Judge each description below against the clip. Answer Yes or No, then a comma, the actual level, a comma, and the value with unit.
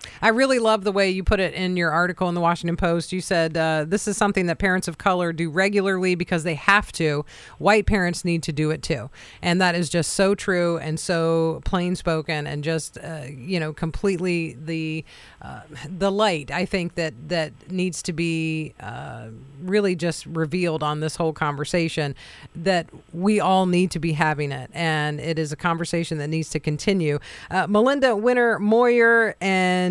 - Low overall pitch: No, medium, 170 Hz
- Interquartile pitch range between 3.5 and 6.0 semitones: No, average, 3.0 semitones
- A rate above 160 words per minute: Yes, average, 190 wpm